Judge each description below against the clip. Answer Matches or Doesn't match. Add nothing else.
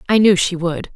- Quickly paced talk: Matches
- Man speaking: Doesn't match